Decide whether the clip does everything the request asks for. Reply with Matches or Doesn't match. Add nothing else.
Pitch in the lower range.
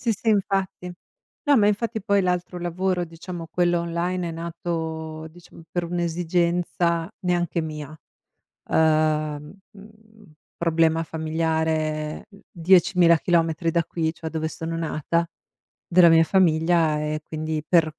Doesn't match